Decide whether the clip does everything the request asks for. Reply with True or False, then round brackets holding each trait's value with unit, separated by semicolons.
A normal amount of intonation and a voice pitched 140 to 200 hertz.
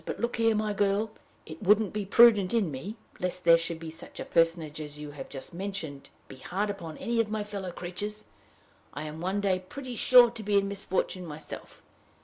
True (4.2 semitones; 190 Hz)